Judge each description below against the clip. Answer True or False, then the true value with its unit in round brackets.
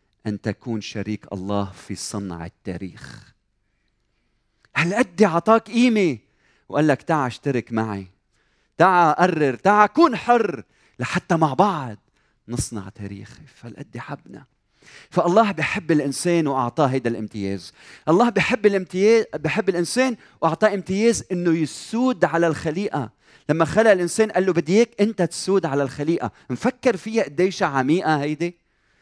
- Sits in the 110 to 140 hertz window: False (155 Hz)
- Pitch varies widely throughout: True (8.8 semitones)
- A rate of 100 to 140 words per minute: True (125 wpm)